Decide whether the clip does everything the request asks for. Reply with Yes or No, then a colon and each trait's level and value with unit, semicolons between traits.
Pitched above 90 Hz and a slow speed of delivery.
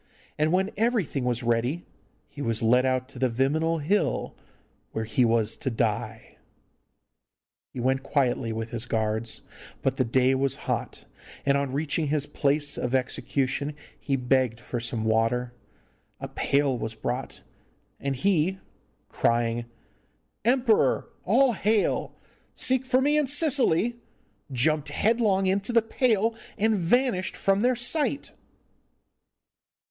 Yes: medium, 140 Hz; slow, 130 wpm